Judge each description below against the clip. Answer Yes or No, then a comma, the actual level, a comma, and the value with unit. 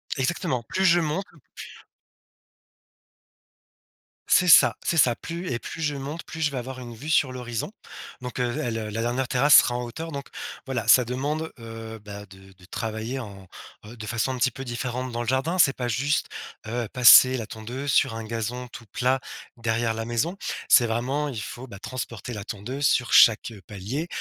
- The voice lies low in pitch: Yes, low, 125 Hz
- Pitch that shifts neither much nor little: Yes, average, 3.3 semitones